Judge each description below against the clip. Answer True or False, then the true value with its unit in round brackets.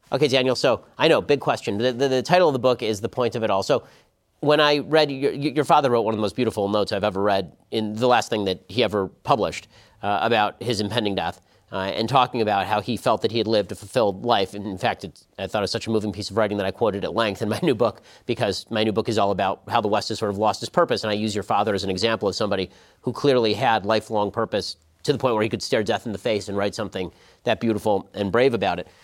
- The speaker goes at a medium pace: False (285 wpm)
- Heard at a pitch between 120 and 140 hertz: False (110 Hz)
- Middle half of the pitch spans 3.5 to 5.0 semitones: False (2.9 semitones)